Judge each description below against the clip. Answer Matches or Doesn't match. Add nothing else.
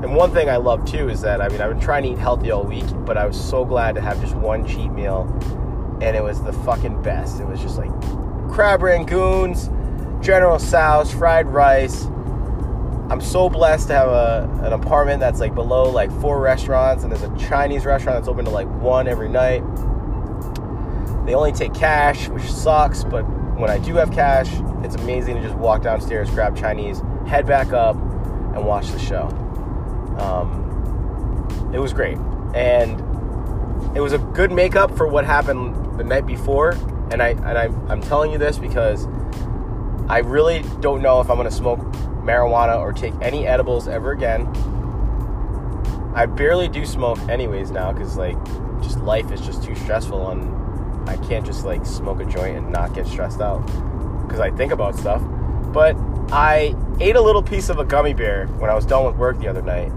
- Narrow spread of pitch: Doesn't match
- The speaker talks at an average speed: Matches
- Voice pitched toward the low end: Matches